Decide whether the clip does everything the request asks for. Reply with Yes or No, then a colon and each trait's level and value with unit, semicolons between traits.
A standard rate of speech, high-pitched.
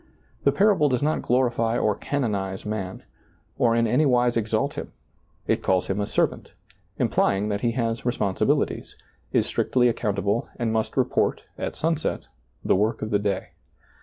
No: average, 155 wpm; low, 115 Hz